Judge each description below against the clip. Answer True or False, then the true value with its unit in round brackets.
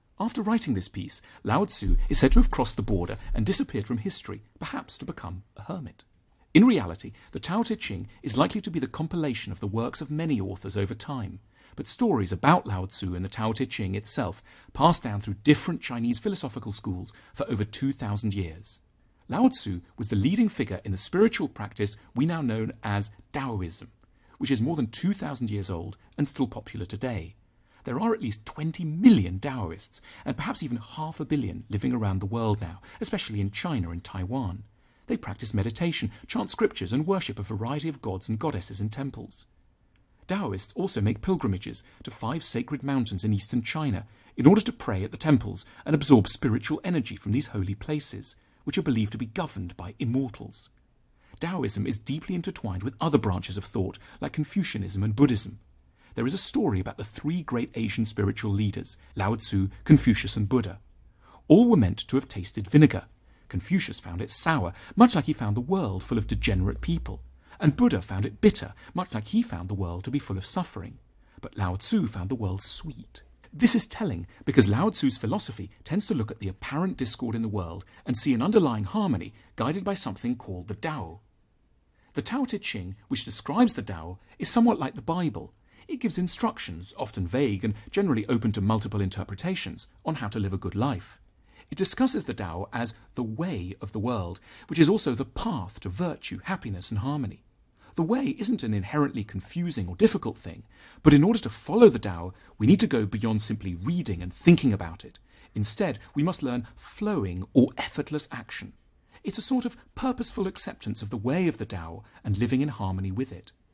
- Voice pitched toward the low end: True (115 Hz)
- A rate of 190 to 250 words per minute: True (195 wpm)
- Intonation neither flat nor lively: False (7.0 semitones)